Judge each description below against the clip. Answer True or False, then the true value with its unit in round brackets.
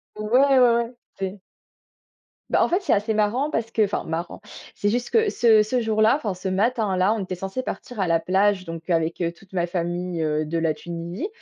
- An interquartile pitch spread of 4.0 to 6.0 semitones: True (5.0 semitones)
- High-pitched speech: True (200 Hz)